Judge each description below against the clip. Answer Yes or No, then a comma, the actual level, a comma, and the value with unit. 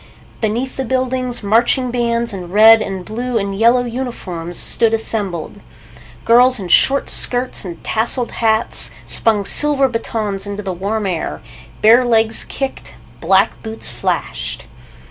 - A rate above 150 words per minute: No, slow, 135 wpm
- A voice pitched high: Yes, high, 225 Hz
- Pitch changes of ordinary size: Yes, average, 3.3 semitones